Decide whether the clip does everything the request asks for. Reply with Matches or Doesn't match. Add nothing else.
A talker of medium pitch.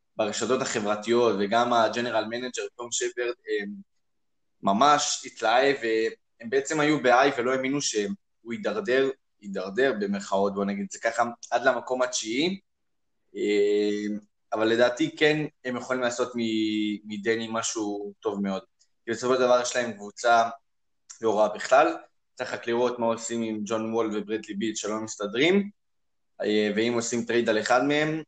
Doesn't match